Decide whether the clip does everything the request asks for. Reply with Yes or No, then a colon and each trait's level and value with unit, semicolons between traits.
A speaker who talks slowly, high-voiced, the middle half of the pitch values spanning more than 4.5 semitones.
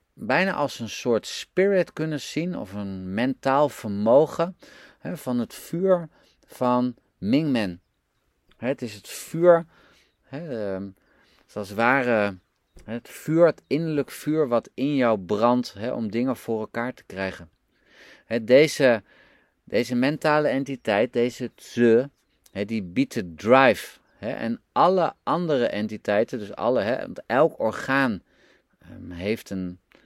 No: slow, 120 wpm; low, 120 Hz; wide, 5.6 semitones